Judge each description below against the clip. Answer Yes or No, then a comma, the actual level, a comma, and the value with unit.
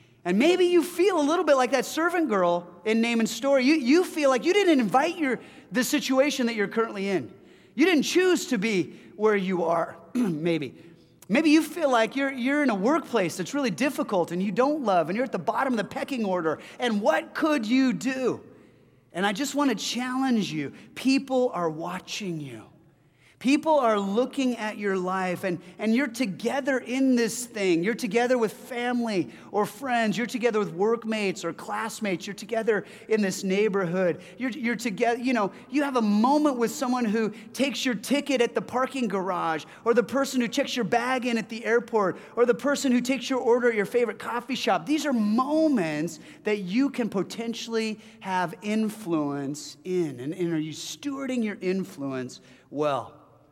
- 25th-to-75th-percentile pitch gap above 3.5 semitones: Yes, wide, 5.6 semitones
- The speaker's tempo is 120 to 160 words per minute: No, average, 190 wpm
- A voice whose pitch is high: Yes, high, 230 Hz